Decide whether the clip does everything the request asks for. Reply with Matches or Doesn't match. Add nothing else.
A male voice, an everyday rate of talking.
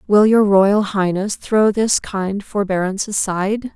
Doesn't match